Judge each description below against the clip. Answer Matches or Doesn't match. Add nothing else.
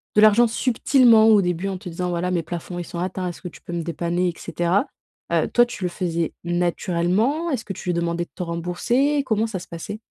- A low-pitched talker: Doesn't match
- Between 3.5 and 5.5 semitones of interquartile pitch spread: Matches